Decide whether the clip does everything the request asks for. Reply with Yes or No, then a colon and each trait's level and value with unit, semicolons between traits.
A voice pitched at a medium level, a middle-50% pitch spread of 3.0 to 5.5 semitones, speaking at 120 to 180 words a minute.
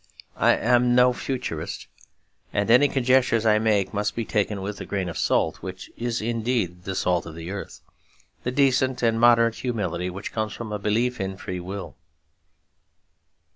No: low, 110 Hz; average, 4.1 semitones; average, 170 wpm